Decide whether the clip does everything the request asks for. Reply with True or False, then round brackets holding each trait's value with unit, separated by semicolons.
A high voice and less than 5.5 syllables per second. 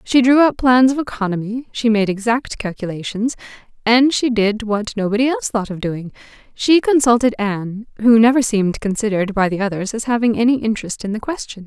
False (225 Hz; 5.7 syllables/s)